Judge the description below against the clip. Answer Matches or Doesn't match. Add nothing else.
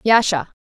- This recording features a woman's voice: Matches